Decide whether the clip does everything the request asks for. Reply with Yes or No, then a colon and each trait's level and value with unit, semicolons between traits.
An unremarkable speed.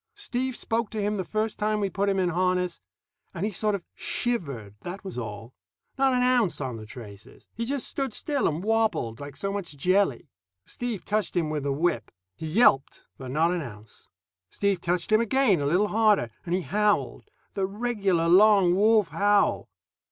Yes: average, 190 wpm